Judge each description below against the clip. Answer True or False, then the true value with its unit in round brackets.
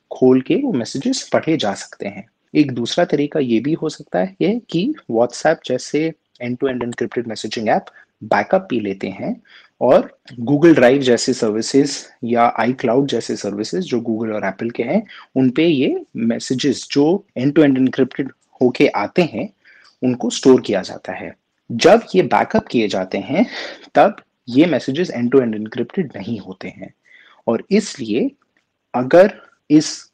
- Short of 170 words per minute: True (160 wpm)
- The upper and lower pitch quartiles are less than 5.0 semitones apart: False (5.4 semitones)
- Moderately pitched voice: False (130 Hz)